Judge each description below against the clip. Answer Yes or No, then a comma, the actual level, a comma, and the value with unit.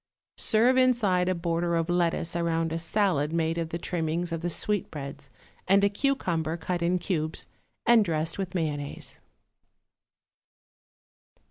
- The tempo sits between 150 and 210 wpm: No, slow, 135 wpm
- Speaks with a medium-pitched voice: Yes, medium, 170 Hz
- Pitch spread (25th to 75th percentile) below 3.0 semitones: Yes, narrow, 2.6 semitones